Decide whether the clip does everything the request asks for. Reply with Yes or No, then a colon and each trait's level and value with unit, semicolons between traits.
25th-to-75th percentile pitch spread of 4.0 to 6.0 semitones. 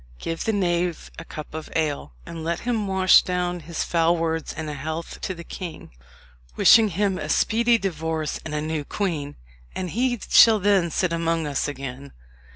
No: average, 3.3 semitones